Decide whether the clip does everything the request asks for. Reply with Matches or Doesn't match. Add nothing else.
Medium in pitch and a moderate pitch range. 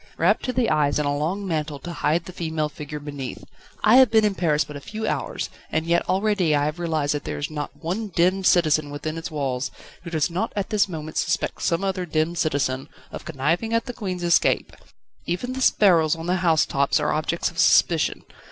Matches